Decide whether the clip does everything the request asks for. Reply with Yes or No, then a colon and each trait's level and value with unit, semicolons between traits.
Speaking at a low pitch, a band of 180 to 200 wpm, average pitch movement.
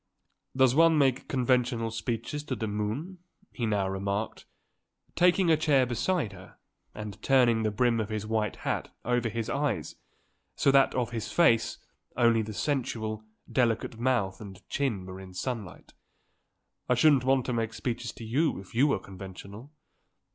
No: low, 115 Hz; average, 160 wpm; average, 3.8 semitones